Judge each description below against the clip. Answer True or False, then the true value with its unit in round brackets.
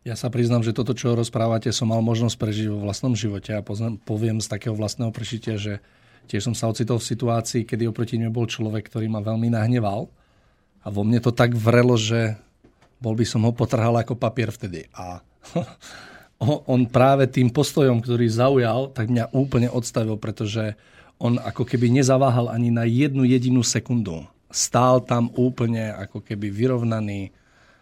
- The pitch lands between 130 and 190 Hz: False (115 Hz)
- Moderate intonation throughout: False (1.9 semitones)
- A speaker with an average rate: False (170 wpm)